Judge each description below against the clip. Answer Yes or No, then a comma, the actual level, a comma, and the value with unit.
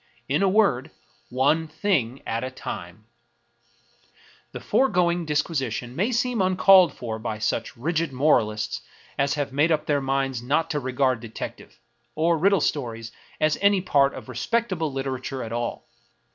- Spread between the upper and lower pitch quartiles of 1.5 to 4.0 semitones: No, average, 5.3 semitones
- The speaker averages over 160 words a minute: No, average, 150 wpm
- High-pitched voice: No, medium, 140 Hz